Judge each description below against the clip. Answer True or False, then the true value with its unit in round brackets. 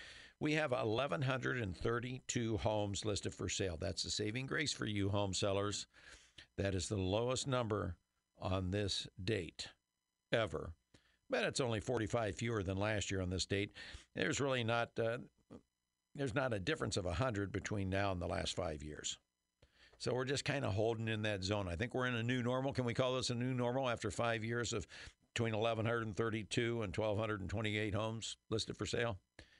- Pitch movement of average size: True (3.4 semitones)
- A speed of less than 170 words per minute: False (175 wpm)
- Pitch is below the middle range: True (110 Hz)